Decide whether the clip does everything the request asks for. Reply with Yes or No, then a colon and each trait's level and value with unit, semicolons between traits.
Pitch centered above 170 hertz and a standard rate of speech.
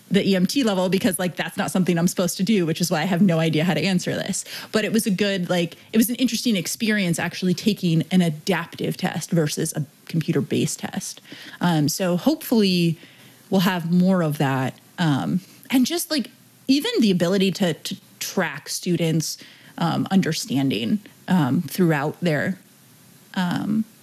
Yes: medium, 185 Hz; average, 170 wpm